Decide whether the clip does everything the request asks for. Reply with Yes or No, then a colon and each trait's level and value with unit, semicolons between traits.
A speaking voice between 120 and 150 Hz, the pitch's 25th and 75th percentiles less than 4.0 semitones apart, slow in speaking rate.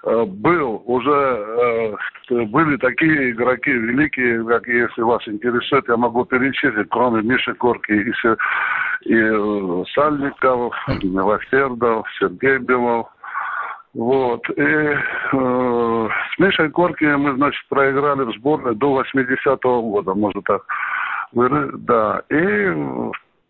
Yes: low, 125 Hz; average, 2.9 semitones; slow, 105 wpm